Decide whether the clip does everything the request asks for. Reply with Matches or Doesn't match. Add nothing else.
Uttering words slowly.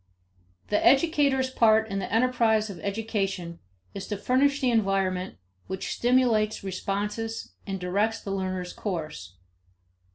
Matches